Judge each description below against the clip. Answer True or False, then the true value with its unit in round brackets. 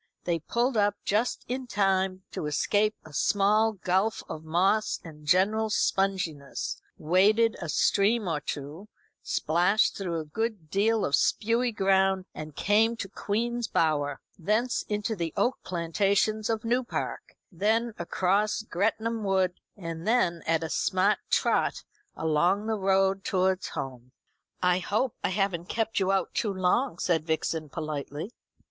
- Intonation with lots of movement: False (4.4 semitones)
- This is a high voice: True (195 Hz)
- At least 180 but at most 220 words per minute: False (145 wpm)